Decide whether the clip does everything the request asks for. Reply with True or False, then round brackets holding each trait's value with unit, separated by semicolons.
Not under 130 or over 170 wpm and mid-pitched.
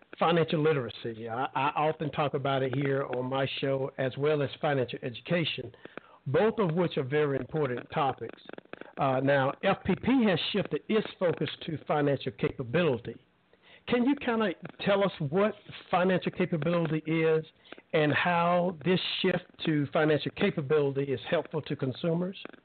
True (145 wpm; 155 Hz)